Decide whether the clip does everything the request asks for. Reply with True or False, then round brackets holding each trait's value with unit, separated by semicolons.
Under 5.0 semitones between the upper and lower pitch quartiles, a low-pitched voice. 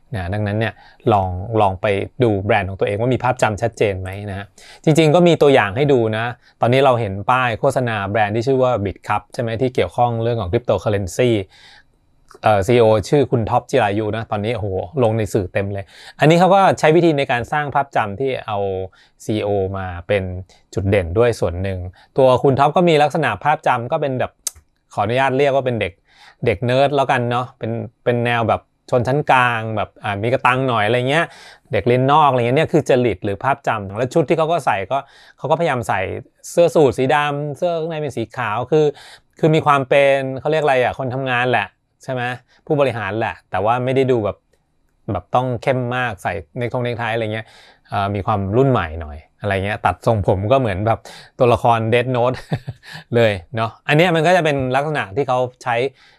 True (4.4 semitones; 120 Hz)